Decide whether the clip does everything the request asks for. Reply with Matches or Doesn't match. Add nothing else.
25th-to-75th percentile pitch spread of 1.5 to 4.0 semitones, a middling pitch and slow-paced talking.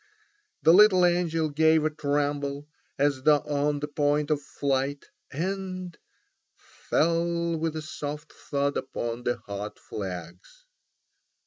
Matches